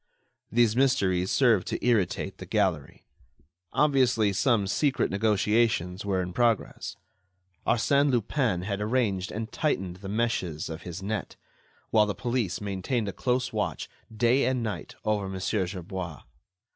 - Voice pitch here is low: Yes, low, 105 Hz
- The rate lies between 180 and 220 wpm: No, slow, 135 wpm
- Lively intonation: No, average, 4.2 semitones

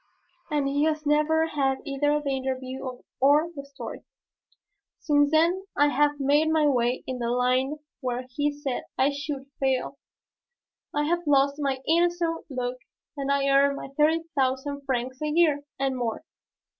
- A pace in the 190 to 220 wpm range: No, average, 155 wpm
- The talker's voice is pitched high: Yes, very high, 280 Hz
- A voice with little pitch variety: Yes, narrow, 2.2 semitones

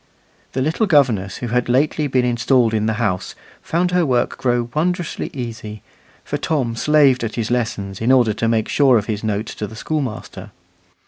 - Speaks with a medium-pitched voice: No, low, 120 Hz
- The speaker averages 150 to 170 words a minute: No, average, 185 wpm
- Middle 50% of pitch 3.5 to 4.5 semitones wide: Yes, average, 4.1 semitones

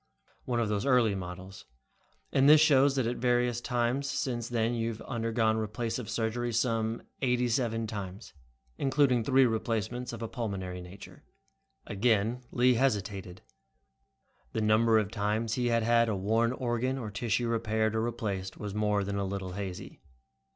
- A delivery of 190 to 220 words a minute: No, average, 160 wpm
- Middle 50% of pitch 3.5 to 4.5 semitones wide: No, average, 2.7 semitones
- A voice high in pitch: No, low, 115 Hz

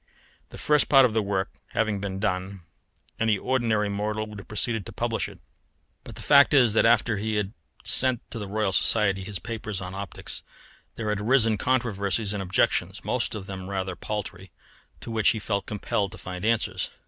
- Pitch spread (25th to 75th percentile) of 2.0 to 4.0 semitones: Yes, narrow, 2.5 semitones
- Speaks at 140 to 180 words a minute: No, average, 190 wpm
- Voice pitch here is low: Yes, low, 105 Hz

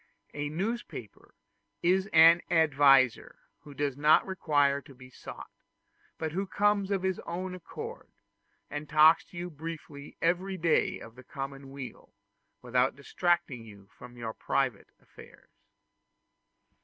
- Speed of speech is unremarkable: No, slow, 130 wpm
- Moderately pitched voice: Yes, medium, 150 Hz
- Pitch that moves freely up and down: No, average, 4.6 semitones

